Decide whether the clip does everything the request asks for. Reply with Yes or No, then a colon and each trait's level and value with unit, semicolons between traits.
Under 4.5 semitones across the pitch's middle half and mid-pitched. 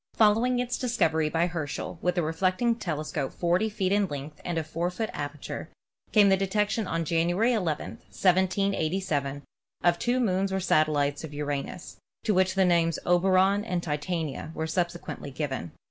Yes: average, 3.9 semitones; medium, 175 Hz